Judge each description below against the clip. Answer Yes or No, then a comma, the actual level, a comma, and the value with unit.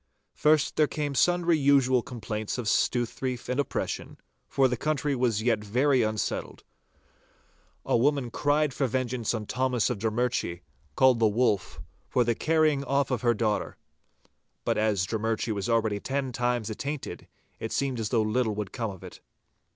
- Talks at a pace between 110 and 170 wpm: Yes, average, 160 wpm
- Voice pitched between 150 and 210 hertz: No, low, 125 Hz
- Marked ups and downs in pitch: No, average, 3.8 semitones